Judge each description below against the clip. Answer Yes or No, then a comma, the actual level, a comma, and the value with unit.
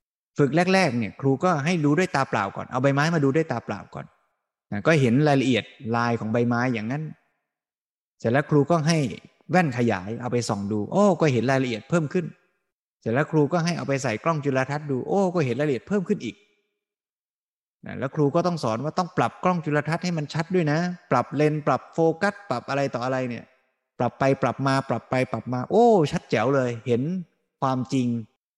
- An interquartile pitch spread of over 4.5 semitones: Yes, wide, 5.4 semitones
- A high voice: No, medium, 140 Hz